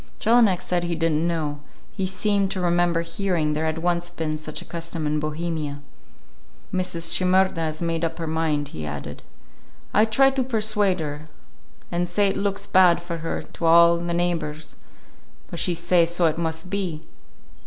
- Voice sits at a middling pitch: Yes, medium, 170 Hz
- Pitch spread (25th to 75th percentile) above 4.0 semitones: No, narrow, 2.4 semitones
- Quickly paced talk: No, average, 175 wpm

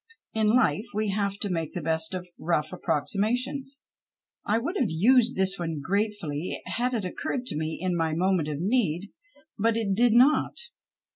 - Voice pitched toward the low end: No, high, 195 Hz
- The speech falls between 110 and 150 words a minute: No, average, 170 wpm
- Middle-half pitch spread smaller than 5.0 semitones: No, wide, 5.6 semitones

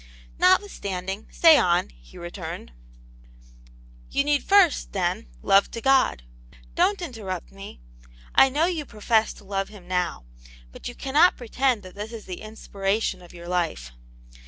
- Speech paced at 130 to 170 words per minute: Yes, average, 155 wpm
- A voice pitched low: No, high, 205 Hz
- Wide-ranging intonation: Yes, wide, 6.8 semitones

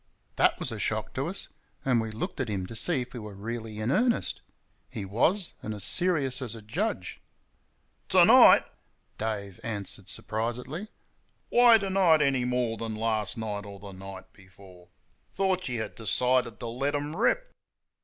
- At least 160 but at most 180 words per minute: Yes, average, 175 wpm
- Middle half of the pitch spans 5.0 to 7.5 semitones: Yes, wide, 5.4 semitones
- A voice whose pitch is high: No, low, 115 Hz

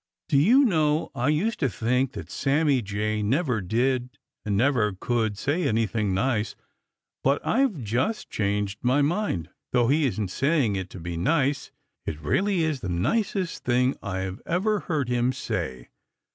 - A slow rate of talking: No, average, 160 wpm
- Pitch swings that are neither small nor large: No, wide, 6.5 semitones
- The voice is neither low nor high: No, low, 125 Hz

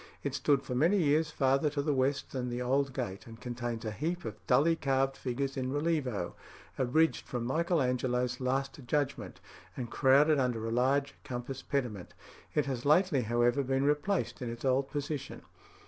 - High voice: No, low, 135 Hz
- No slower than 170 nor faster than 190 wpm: Yes, average, 175 wpm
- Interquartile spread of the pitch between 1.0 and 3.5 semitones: Yes, average, 2.8 semitones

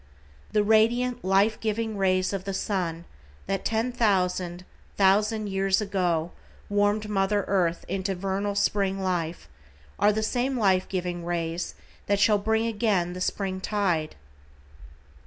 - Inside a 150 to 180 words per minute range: No, slow, 135 wpm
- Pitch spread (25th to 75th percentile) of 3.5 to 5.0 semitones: No, narrow, 2.5 semitones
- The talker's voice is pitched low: No, high, 195 Hz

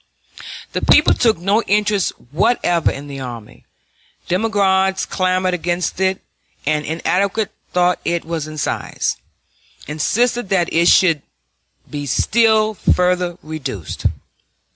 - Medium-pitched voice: Yes, medium, 180 Hz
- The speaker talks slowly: Yes, slow, 115 wpm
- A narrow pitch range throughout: No, average, 4.1 semitones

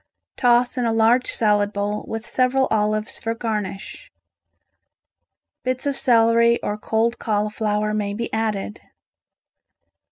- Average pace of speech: No, slow, 120 wpm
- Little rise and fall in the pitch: Yes, narrow, 2.1 semitones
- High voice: Yes, high, 225 Hz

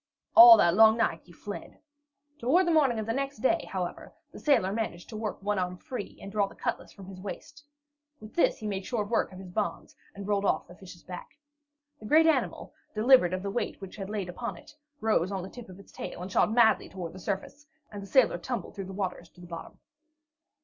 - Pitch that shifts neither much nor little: Yes, average, 4.0 semitones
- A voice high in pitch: Yes, high, 205 Hz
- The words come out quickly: Yes, fast, 230 wpm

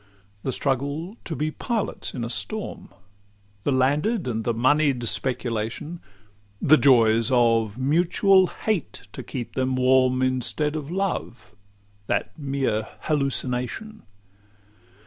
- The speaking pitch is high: No, low, 135 Hz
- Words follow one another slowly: Yes, slow, 115 wpm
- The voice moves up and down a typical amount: Yes, average, 4.0 semitones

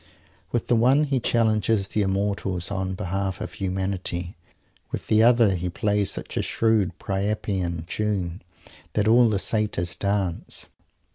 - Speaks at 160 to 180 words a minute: No, average, 140 wpm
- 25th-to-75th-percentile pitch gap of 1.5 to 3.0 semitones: Yes, average, 2.7 semitones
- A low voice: Yes, low, 100 Hz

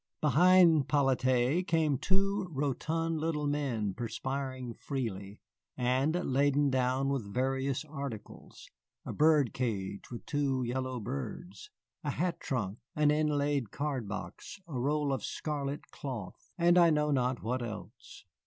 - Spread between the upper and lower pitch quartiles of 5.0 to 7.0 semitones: No, average, 3.3 semitones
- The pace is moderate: No, slow, 130 wpm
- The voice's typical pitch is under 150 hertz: Yes, low, 135 Hz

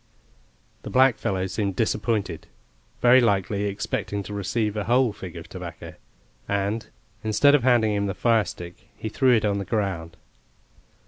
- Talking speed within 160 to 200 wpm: No, average, 145 wpm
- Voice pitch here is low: Yes, low, 105 Hz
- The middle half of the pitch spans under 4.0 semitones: Yes, average, 2.9 semitones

